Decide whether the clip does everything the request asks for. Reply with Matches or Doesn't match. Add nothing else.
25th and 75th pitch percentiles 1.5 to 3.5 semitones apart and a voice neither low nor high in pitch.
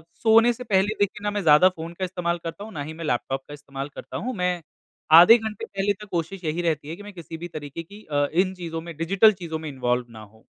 Doesn't match